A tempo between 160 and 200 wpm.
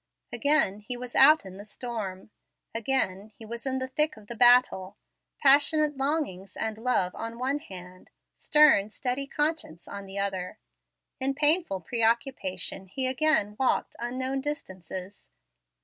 No: average, 145 wpm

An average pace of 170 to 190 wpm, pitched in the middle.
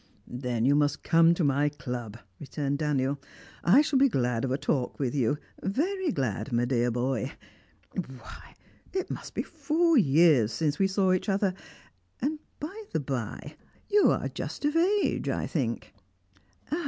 No: average, 160 wpm; medium, 145 Hz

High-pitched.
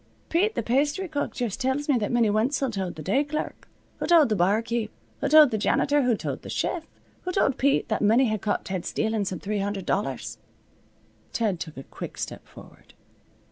Yes: high, 230 Hz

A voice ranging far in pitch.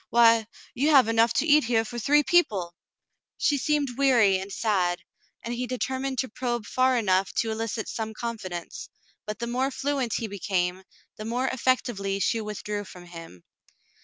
No: average, 4.2 semitones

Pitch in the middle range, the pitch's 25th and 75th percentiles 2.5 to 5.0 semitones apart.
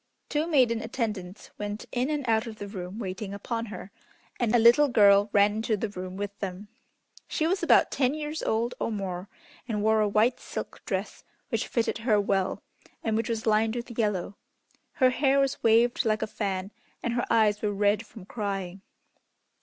No: high, 220 Hz; average, 2.8 semitones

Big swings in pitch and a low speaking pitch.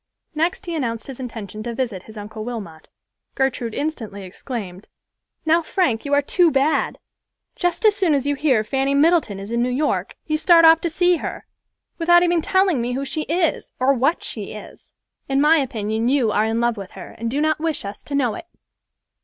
No: wide, 6.1 semitones; very high, 270 Hz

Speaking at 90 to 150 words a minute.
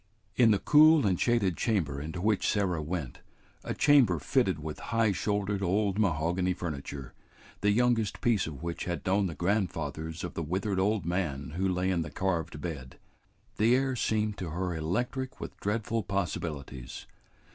No: average, 165 wpm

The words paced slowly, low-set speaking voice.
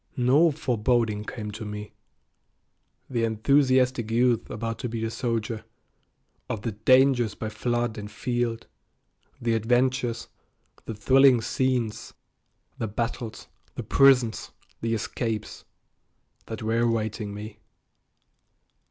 Yes: slow, 110 wpm; low, 115 Hz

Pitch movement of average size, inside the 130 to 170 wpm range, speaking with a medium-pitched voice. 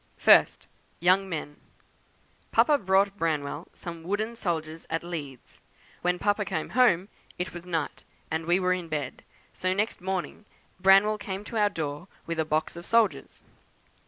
Yes: average, 3.5 semitones; average, 155 wpm; medium, 180 Hz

